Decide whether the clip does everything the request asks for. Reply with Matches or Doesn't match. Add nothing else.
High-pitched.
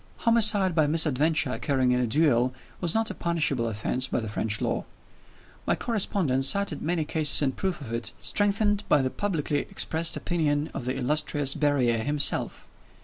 Doesn't match